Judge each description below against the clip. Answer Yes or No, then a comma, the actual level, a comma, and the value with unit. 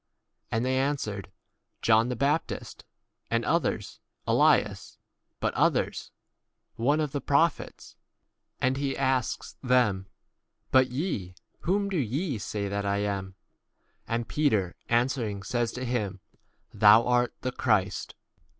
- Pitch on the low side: Yes, low, 120 Hz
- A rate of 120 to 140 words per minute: Yes, slow, 135 wpm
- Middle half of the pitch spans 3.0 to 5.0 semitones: Yes, average, 4.7 semitones